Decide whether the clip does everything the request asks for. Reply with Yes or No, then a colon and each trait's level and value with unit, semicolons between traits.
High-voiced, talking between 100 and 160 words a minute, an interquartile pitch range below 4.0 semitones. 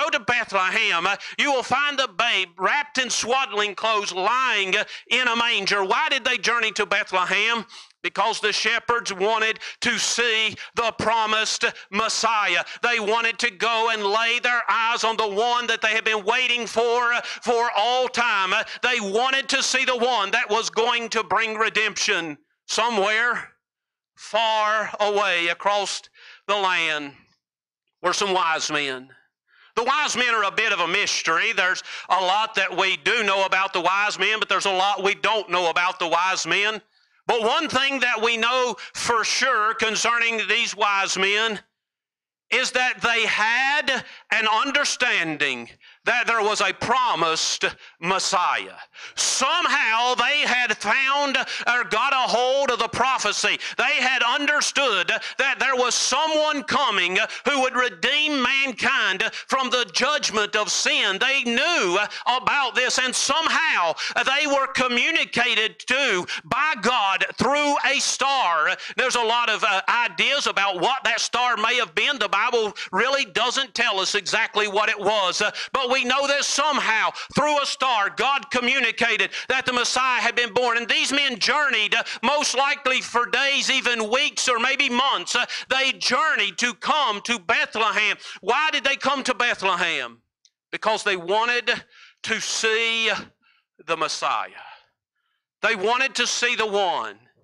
Yes: high, 235 Hz; average, 150 wpm; average, 3.6 semitones